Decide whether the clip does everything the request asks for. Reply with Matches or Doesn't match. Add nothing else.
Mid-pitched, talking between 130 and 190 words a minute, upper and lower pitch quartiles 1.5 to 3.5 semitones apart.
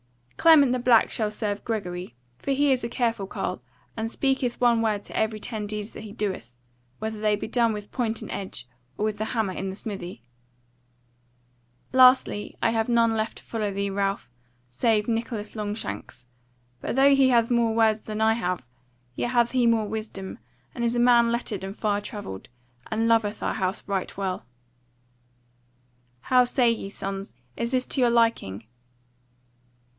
Doesn't match